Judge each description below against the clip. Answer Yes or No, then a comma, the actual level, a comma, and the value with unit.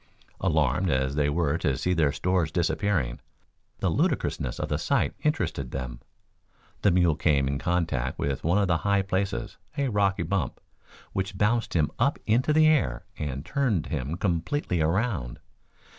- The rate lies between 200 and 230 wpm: No, average, 160 wpm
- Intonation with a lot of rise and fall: Yes, wide, 5.8 semitones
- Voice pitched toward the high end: No, very low, 85 Hz